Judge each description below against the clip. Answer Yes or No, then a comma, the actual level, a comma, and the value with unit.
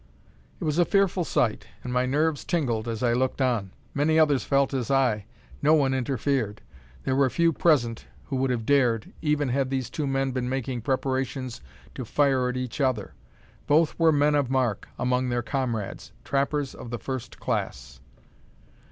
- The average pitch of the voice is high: No, low, 130 Hz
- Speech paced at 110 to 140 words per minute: No, average, 175 wpm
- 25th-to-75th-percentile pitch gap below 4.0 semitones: Yes, average, 2.8 semitones